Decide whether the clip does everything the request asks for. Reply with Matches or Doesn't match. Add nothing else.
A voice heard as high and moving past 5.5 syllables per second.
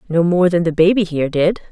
Doesn't match